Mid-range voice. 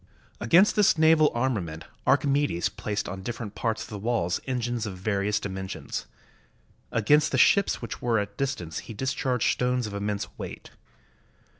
No: low, 115 Hz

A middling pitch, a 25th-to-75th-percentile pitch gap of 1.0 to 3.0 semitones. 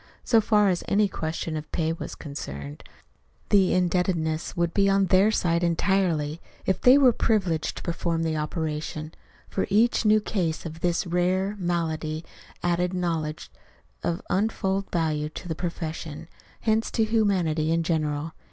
No: medium, 170 Hz; average, 3.5 semitones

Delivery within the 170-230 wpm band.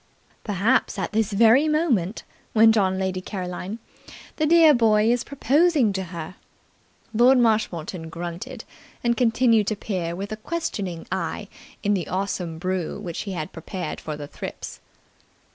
No: average, 145 wpm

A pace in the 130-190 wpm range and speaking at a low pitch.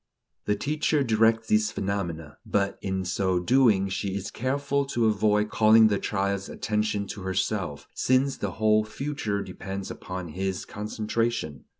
Yes: average, 140 wpm; low, 105 Hz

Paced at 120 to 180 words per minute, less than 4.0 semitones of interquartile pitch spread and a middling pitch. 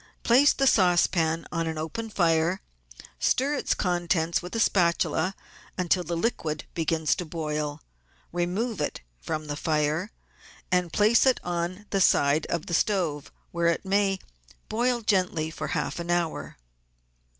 Yes: average, 145 wpm; average, 3.6 semitones; medium, 175 Hz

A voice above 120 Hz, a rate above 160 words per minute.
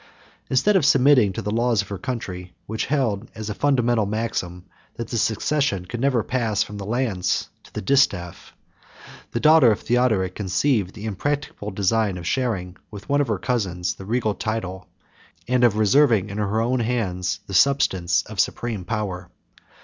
No: low, 110 Hz; average, 170 wpm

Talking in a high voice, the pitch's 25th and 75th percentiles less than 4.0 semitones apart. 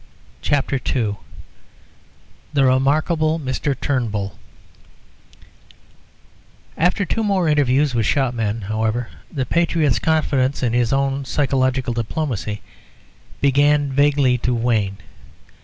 No: low, 135 Hz; average, 3.6 semitones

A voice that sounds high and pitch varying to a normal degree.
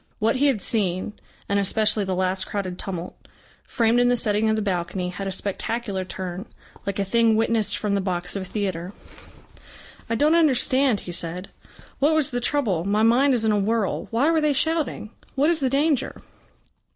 Yes: high, 215 Hz; average, 4.9 semitones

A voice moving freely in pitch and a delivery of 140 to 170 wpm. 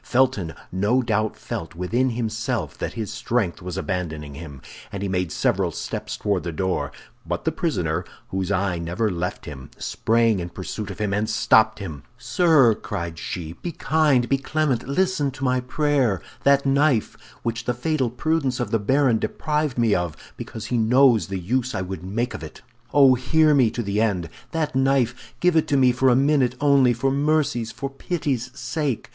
No: wide, 5.8 semitones; average, 185 wpm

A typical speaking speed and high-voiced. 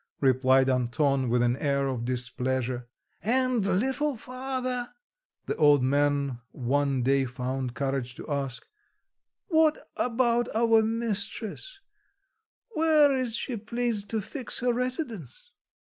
No: slow, 115 wpm; high, 195 Hz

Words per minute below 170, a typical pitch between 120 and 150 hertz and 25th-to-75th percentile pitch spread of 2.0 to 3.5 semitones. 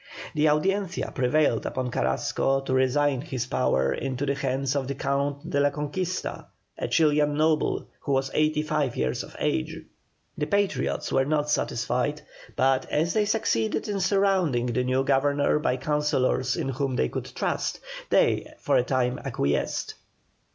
Yes: average, 160 wpm; medium, 140 Hz; average, 2.8 semitones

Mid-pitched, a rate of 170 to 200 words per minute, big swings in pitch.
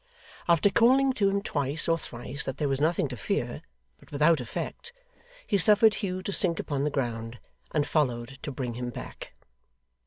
Yes: medium, 150 Hz; average, 180 wpm; wide, 7.0 semitones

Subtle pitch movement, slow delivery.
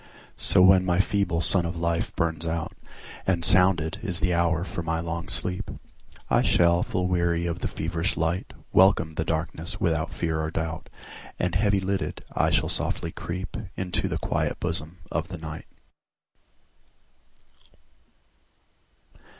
Yes: narrow, 2.0 semitones; slow, 130 wpm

